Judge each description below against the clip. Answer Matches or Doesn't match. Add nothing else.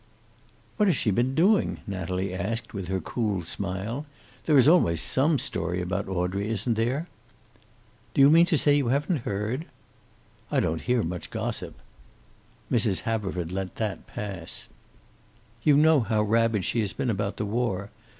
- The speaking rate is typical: Matches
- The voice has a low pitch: Matches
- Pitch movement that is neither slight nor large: Doesn't match